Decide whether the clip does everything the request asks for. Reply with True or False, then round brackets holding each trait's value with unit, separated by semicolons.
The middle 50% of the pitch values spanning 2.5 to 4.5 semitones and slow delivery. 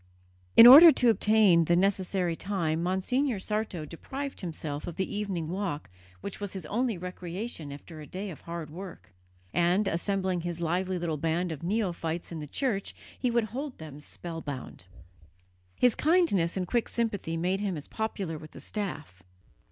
False (4.2 semitones; 165 wpm)